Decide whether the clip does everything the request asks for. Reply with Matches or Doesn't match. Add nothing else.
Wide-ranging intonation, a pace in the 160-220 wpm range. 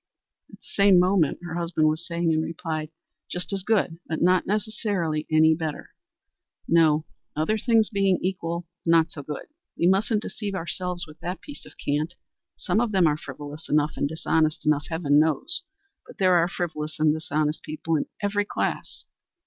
Doesn't match